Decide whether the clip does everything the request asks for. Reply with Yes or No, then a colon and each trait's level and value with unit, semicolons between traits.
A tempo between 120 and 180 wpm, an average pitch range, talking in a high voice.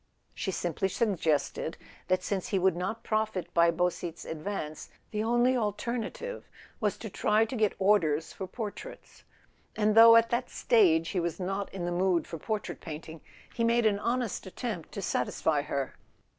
Yes: average, 170 wpm; average, 4.7 semitones; high, 195 Hz